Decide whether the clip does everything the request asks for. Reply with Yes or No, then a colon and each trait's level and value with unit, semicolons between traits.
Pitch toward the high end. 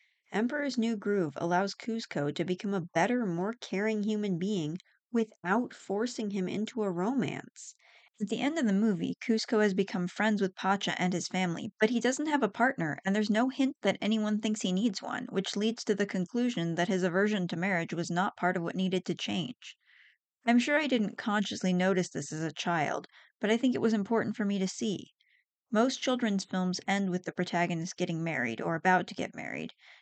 Yes: high, 200 Hz